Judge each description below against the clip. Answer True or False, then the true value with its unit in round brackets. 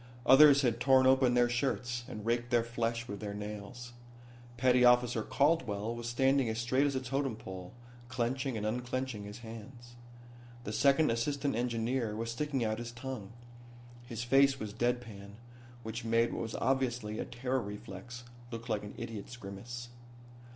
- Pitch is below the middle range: True (120 Hz)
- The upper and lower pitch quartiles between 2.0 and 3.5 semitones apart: True (2.6 semitones)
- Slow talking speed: False (160 wpm)